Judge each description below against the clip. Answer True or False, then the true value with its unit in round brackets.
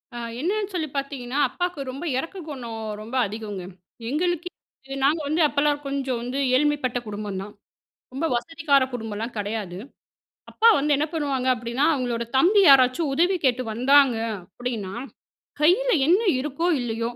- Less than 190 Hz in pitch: False (270 Hz)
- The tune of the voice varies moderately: True (4.5 semitones)